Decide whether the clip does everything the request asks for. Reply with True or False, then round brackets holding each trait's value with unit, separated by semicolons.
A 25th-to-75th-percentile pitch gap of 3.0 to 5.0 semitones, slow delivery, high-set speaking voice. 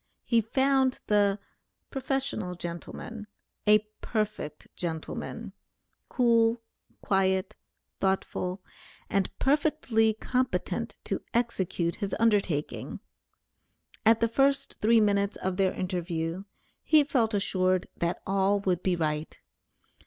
True (3.9 semitones; 100 wpm; 205 Hz)